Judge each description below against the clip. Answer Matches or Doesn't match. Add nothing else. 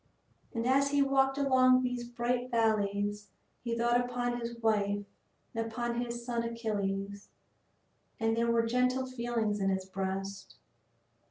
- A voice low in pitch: Doesn't match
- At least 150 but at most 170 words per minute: Doesn't match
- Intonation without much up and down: Doesn't match